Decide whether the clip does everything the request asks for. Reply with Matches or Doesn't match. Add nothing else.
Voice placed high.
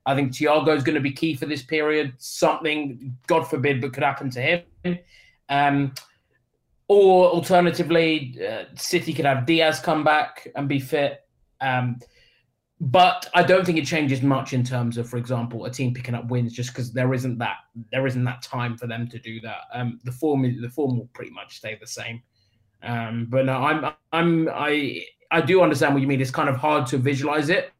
Doesn't match